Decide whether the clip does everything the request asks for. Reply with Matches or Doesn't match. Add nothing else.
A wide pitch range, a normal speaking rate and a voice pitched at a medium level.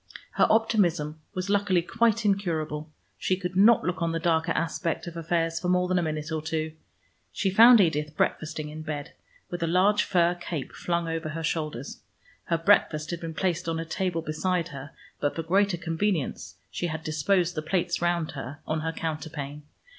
Doesn't match